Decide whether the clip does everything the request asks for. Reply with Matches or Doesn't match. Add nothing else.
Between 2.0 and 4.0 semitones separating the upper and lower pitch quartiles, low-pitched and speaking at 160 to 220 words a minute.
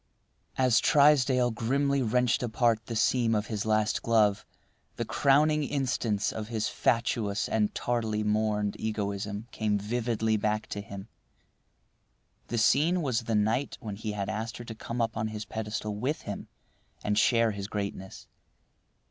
Doesn't match